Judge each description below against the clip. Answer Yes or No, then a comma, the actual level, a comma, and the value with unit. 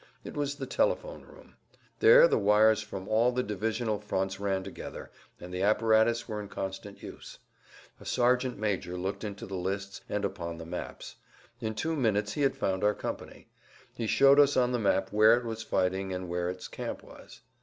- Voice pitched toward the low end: Yes, low, 105 Hz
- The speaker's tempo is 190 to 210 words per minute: Yes, average, 195 wpm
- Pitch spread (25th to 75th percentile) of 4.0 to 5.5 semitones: Yes, average, 4.3 semitones